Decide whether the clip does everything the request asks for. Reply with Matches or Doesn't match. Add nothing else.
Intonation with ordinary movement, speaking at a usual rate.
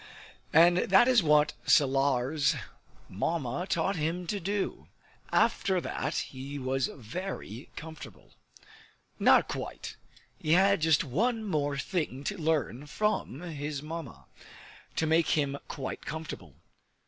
Doesn't match